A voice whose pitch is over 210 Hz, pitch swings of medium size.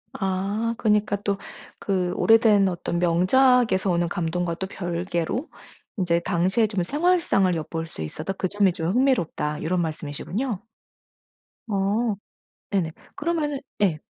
No: high, 190 Hz; average, 4.2 semitones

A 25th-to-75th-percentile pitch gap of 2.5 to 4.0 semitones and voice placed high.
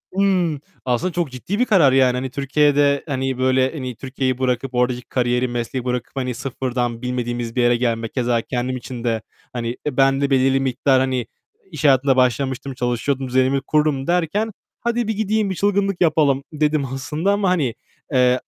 No: average, 3.2 semitones; low, 130 Hz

